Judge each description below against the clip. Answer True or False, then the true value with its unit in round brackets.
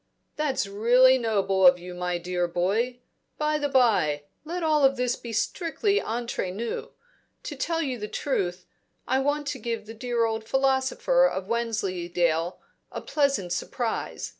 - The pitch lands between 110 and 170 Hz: False (235 Hz)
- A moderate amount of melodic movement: False (6.1 semitones)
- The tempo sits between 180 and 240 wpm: False (155 wpm)